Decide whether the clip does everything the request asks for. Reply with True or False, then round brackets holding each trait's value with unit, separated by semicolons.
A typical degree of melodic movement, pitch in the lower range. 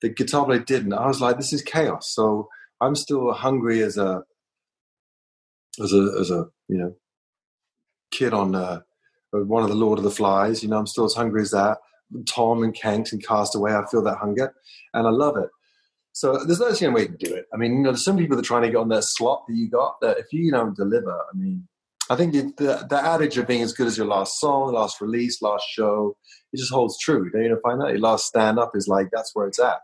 True (4.4 semitones; 115 Hz)